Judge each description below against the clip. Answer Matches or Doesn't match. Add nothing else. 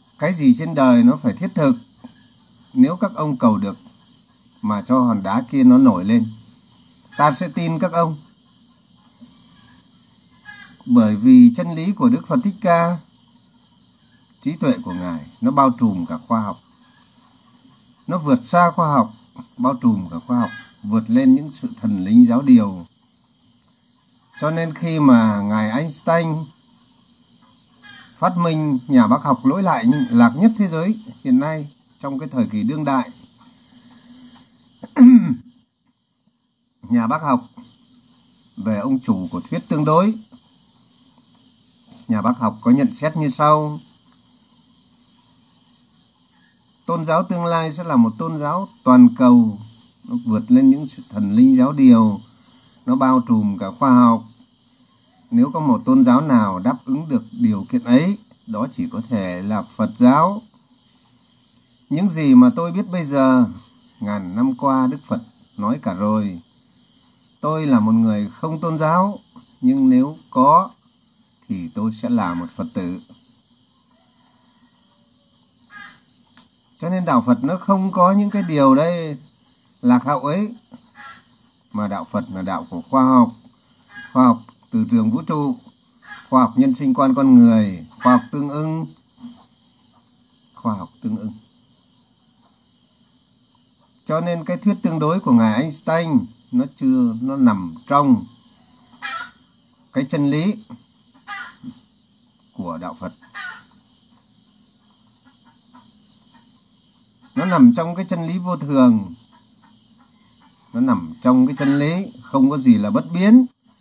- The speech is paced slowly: Matches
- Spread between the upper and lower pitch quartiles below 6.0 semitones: Doesn't match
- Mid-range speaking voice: Doesn't match